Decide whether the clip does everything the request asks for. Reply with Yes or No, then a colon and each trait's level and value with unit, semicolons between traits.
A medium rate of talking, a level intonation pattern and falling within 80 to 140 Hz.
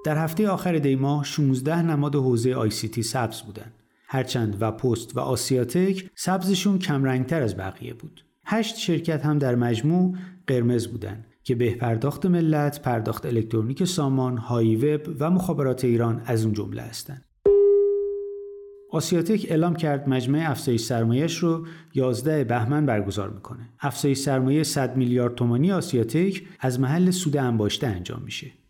No: average, 145 wpm; wide, 5.6 semitones; low, 135 Hz